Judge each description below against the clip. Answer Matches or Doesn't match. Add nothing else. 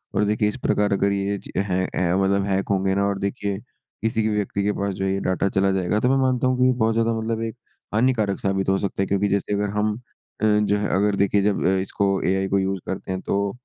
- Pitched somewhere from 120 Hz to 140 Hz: Doesn't match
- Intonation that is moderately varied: Doesn't match